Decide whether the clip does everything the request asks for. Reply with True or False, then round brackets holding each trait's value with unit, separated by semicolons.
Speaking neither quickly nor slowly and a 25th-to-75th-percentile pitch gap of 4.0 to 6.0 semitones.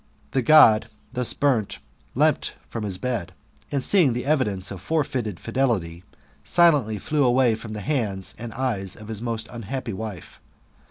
True (160 wpm; 4.3 semitones)